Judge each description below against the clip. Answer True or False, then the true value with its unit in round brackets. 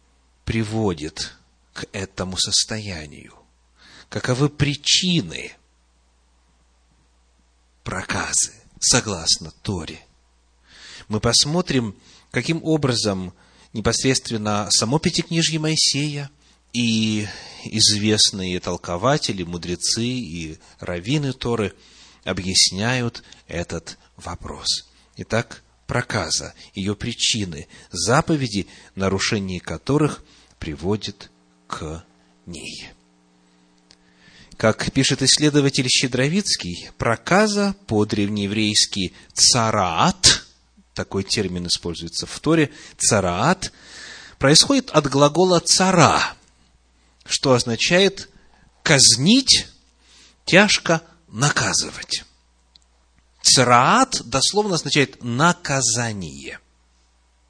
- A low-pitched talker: True (105 Hz)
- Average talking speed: False (65 wpm)